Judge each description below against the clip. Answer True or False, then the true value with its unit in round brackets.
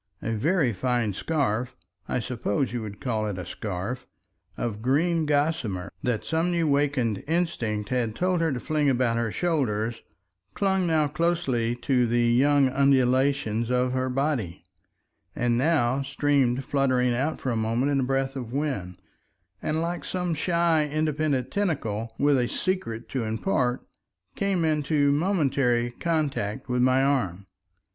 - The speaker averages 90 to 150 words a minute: True (145 wpm)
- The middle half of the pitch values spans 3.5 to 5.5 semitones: True (4.5 semitones)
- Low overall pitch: True (130 Hz)